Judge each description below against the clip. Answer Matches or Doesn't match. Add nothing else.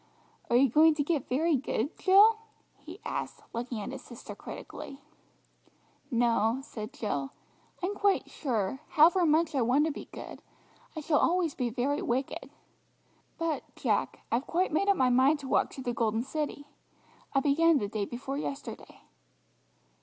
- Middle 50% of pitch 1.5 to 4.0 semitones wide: Doesn't match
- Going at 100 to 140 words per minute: Doesn't match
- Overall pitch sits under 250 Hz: Doesn't match